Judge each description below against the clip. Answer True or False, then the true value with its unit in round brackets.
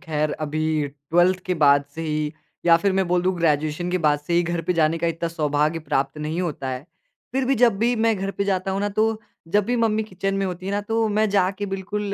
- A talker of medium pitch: True (180 Hz)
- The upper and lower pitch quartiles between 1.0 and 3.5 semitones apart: False (4.6 semitones)